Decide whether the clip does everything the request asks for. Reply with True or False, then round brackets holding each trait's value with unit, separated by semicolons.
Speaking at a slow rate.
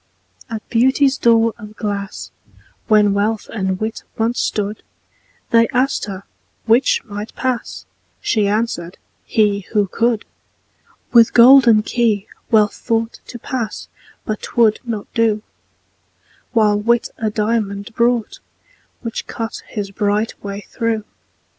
True (120 wpm)